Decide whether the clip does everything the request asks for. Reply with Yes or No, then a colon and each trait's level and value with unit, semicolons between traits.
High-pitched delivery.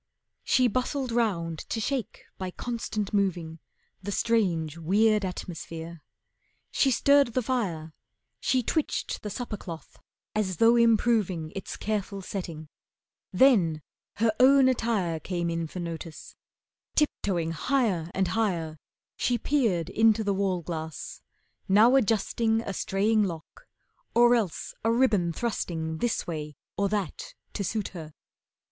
Yes: high, 200 Hz